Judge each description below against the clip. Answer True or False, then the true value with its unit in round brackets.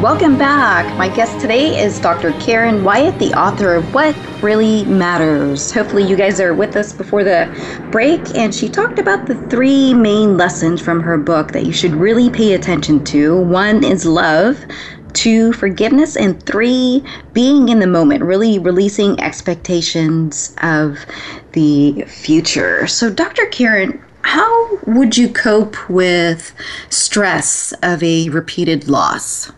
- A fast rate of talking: False (145 wpm)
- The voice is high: True (195 Hz)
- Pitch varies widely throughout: True (5.8 semitones)